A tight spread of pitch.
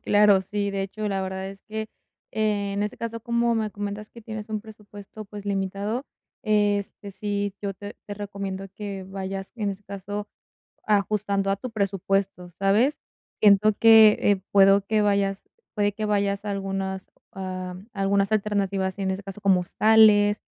Yes: narrow, 1.4 semitones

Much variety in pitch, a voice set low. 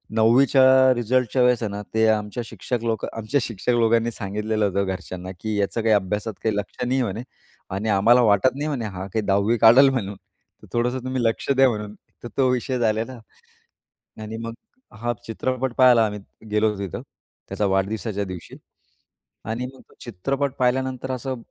No: average, 3.4 semitones; low, 115 Hz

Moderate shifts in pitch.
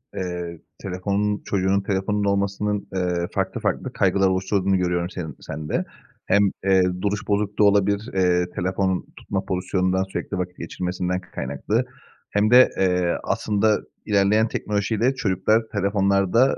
No: narrow, 2.0 semitones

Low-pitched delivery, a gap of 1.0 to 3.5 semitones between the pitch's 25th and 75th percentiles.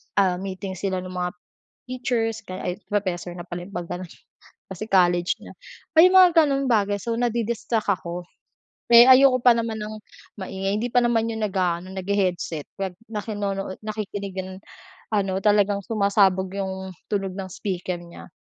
No: high, 200 Hz; average, 3.2 semitones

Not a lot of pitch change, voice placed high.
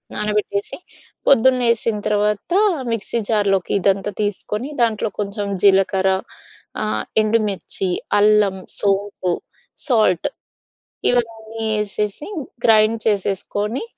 Yes: narrow, 1.9 semitones; high, 210 Hz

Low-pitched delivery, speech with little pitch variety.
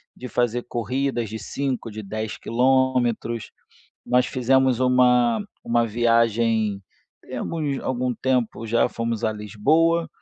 Yes: low, 120 Hz; narrow, 2.3 semitones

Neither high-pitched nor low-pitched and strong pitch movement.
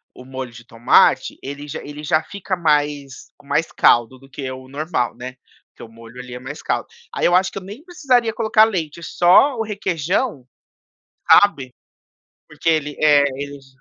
Yes: medium, 145 Hz; wide, 6.1 semitones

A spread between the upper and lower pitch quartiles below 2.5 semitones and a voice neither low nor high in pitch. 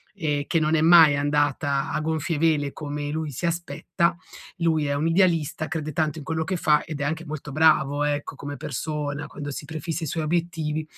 Yes: narrow, 1.9 semitones; medium, 155 Hz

